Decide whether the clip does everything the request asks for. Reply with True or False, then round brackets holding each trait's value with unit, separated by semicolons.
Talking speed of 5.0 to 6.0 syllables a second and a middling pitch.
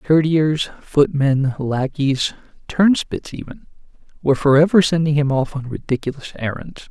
False (4.7 syllables/s; 145 Hz)